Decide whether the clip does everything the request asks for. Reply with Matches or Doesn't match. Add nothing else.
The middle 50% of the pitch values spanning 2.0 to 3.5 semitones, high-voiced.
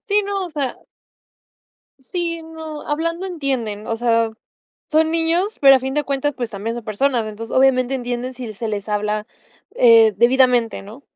Doesn't match